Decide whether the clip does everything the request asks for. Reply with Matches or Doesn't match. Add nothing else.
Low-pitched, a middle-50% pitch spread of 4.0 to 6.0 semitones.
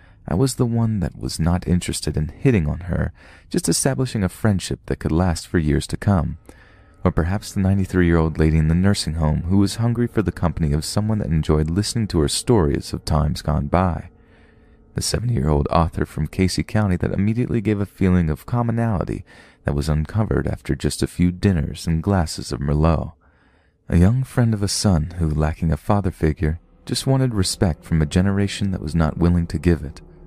Matches